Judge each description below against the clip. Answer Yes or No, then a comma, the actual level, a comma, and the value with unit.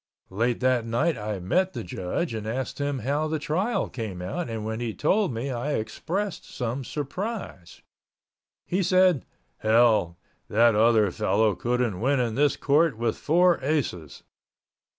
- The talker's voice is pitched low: Yes, low, 125 Hz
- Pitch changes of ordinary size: No, wide, 5.8 semitones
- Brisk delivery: No, average, 150 wpm